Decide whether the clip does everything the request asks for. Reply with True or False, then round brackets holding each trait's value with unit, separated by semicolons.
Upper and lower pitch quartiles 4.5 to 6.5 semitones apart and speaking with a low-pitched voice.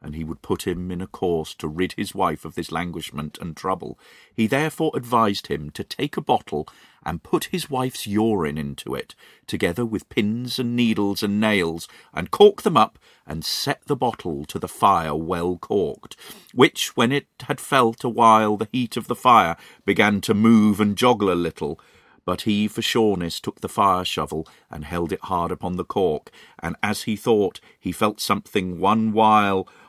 True (4.9 semitones; 105 Hz)